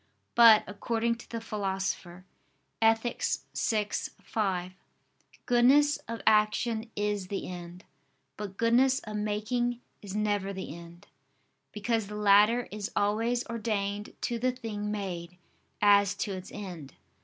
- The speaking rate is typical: No, slow, 125 wpm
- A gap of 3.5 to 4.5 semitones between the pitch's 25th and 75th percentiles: No, average, 2.8 semitones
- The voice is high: Yes, high, 210 Hz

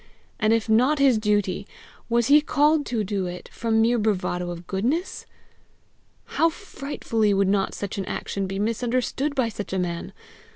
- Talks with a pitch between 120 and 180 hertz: No, high, 220 Hz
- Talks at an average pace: Yes, average, 165 wpm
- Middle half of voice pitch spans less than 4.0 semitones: No, average, 4.7 semitones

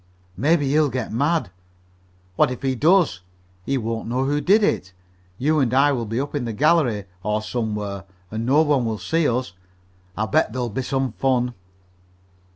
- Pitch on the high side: No, low, 130 Hz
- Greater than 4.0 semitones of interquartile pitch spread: Yes, average, 4.6 semitones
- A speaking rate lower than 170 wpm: No, average, 175 wpm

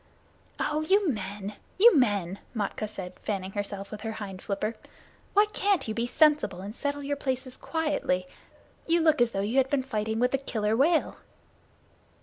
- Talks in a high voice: Yes, high, 230 Hz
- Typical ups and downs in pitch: No, wide, 6.0 semitones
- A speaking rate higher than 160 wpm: Yes, average, 170 wpm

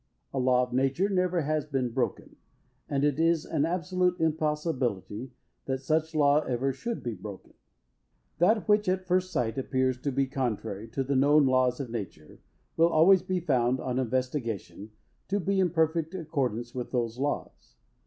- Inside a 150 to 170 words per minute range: Yes, average, 165 wpm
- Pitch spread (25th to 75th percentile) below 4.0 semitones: No, average, 4.8 semitones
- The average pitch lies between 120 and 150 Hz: Yes, medium, 140 Hz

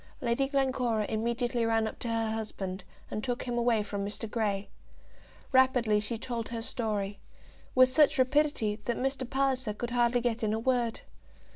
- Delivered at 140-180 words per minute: Yes, average, 165 wpm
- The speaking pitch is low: No, high, 235 Hz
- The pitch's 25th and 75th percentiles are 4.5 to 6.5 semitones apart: No, average, 2.7 semitones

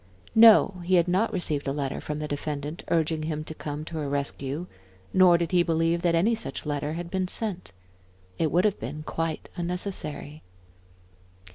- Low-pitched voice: No, medium, 165 Hz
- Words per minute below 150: No, average, 175 wpm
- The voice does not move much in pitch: No, average, 3.1 semitones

